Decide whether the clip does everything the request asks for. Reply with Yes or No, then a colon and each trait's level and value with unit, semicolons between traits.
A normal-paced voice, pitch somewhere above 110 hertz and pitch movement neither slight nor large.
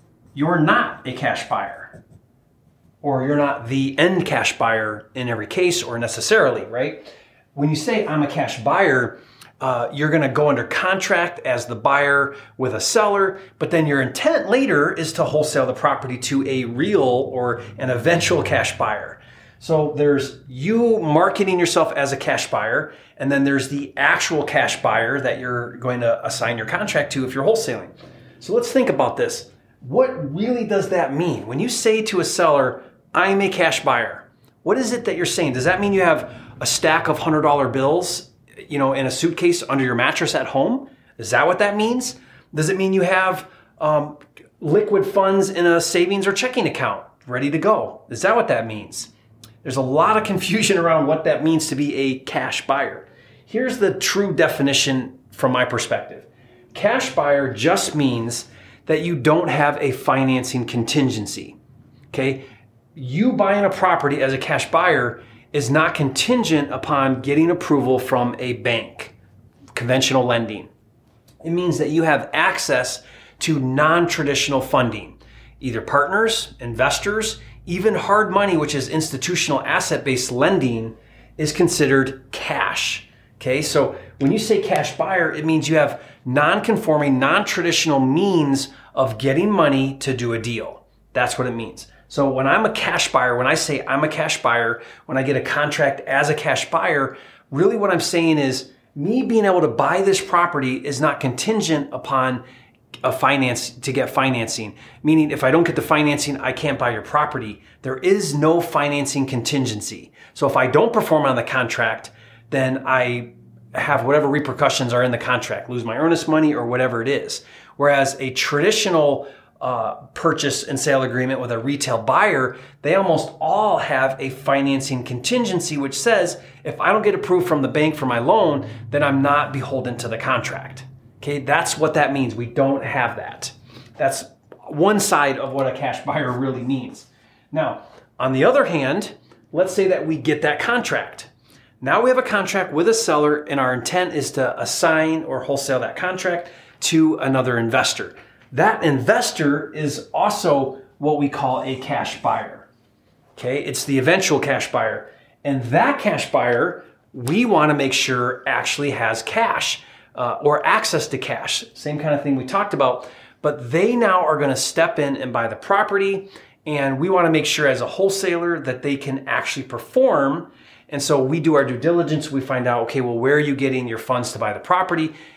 Yes: average, 180 wpm; medium, 140 Hz; average, 4.4 semitones